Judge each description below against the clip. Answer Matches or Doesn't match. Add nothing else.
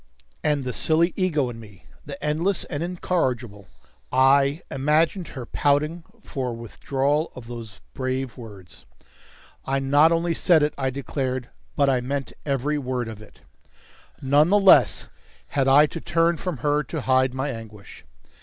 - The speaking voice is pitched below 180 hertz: Matches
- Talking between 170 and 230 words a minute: Doesn't match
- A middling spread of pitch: Matches